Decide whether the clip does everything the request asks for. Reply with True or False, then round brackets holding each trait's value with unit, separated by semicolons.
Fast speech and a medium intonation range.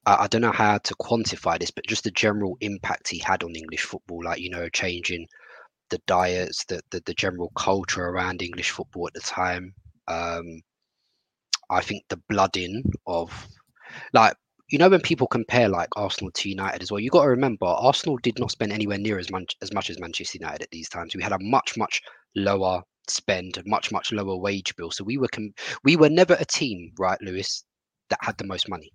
True (210 wpm; 3.4 semitones)